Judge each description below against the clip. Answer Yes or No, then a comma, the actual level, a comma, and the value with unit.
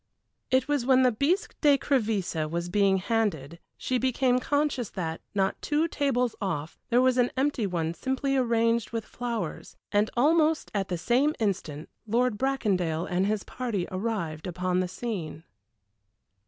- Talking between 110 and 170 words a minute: Yes, average, 150 wpm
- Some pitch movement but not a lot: No, wide, 6.0 semitones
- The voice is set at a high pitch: Yes, high, 225 Hz